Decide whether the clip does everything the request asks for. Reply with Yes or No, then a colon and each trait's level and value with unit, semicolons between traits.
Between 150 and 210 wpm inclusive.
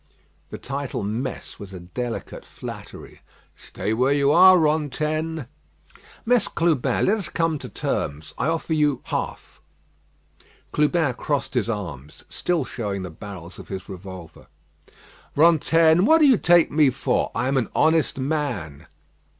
No: average, 140 wpm